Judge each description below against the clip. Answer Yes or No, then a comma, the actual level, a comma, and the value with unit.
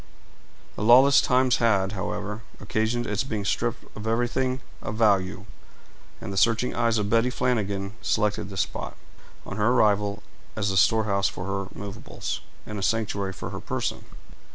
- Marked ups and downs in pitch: No, average, 2.7 semitones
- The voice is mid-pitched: No, low, 105 Hz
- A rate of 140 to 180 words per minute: Yes, average, 155 wpm